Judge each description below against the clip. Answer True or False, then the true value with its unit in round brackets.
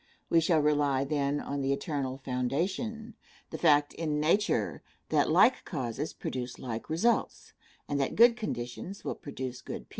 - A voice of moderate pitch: True (145 Hz)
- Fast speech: False (155 wpm)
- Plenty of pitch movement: False (4.1 semitones)